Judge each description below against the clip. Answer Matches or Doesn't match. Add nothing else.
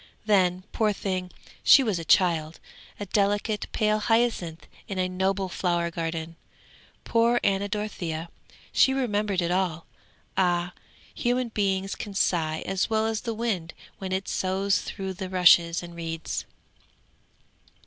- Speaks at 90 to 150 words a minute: Matches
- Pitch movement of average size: Matches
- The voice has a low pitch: Doesn't match